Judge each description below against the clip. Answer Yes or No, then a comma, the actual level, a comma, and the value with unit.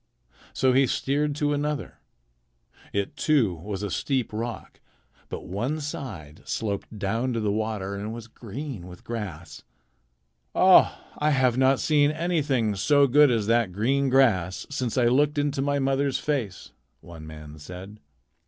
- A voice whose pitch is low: Yes, low, 120 Hz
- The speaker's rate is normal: Yes, average, 150 wpm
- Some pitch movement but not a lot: No, wide, 5.8 semitones